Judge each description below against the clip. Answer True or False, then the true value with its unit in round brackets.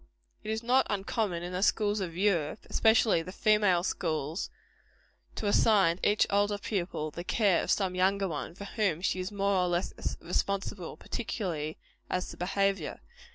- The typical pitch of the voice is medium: False (195 Hz)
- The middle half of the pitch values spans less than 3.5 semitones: True (2.9 semitones)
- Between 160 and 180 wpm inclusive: True (165 wpm)